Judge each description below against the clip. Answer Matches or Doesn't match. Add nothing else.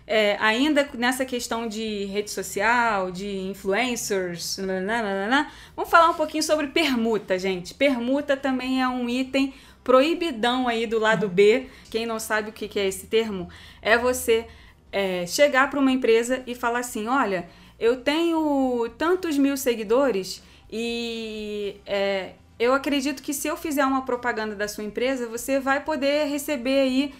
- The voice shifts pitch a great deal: Doesn't match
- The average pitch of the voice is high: Matches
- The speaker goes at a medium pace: Matches